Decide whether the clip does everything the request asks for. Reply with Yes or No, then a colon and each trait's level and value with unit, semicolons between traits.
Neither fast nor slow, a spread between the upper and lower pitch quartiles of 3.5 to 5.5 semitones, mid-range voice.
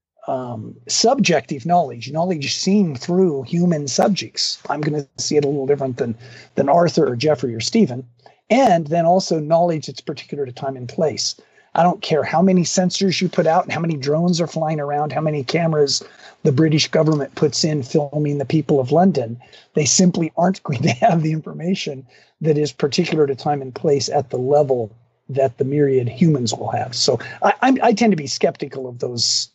Yes: average, 195 wpm; average, 3.8 semitones; medium, 155 Hz